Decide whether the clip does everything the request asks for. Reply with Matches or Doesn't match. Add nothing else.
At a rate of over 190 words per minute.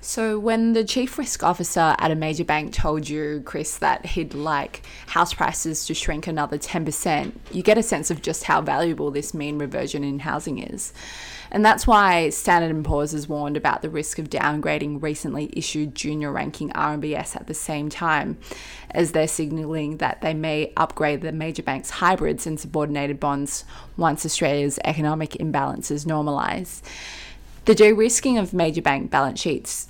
Doesn't match